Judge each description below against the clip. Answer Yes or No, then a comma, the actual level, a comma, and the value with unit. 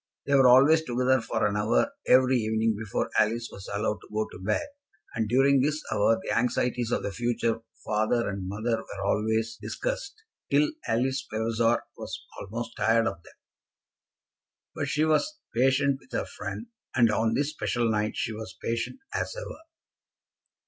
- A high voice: No, low, 115 Hz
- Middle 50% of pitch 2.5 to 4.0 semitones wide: Yes, average, 3.3 semitones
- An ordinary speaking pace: Yes, average, 165 wpm